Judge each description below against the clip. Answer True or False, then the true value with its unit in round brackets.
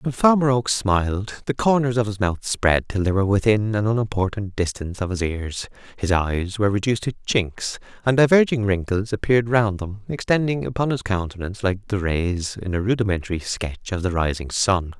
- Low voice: True (105 Hz)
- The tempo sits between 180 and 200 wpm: True (190 wpm)